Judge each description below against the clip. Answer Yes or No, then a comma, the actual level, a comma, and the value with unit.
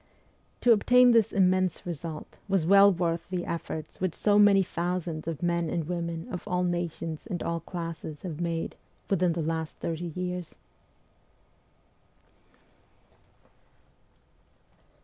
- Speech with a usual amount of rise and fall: No, narrow, 1.9 semitones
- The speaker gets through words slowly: Yes, slow, 125 wpm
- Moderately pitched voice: Yes, medium, 175 Hz